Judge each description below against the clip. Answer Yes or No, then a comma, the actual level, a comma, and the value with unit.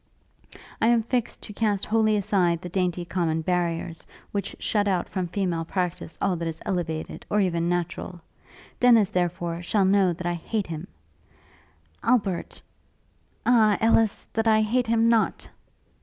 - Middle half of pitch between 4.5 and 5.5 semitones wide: No, average, 3.9 semitones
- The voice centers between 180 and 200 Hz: Yes, high, 190 Hz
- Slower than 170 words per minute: Yes, average, 150 wpm